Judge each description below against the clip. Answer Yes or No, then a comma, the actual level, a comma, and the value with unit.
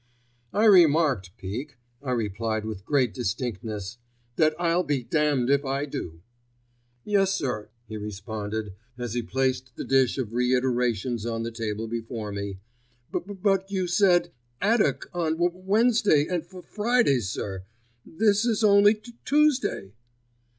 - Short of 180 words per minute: Yes, average, 155 wpm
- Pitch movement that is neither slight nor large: No, wide, 8.6 semitones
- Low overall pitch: Yes, low, 130 Hz